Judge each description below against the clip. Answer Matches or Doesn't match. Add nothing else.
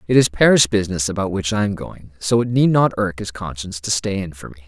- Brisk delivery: Matches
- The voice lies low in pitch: Matches